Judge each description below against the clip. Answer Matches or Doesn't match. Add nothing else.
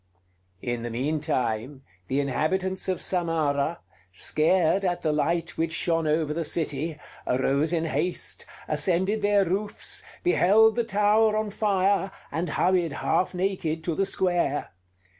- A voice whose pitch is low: Doesn't match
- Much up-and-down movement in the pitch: Doesn't match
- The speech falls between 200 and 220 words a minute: Doesn't match